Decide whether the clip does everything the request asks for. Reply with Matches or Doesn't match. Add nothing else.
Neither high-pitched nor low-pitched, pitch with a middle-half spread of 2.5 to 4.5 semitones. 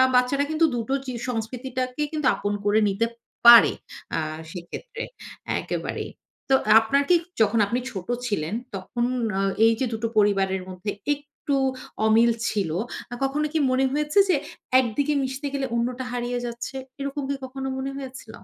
Doesn't match